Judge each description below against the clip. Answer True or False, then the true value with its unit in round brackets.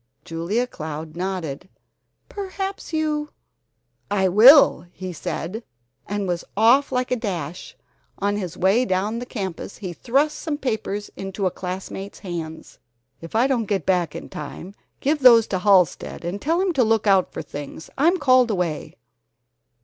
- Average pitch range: False (5.9 semitones)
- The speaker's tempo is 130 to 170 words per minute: True (155 wpm)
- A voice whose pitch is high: True (200 Hz)